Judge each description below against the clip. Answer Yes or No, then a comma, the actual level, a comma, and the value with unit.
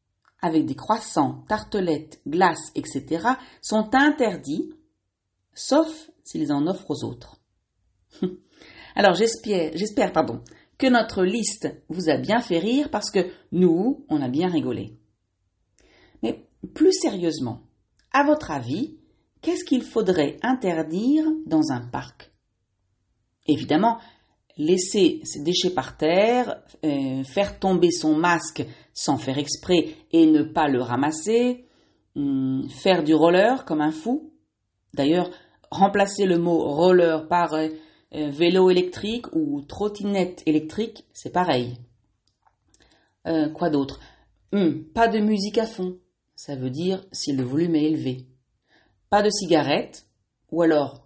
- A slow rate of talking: Yes, slow, 125 wpm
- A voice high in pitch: No, medium, 175 Hz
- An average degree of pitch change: No, wide, 7.2 semitones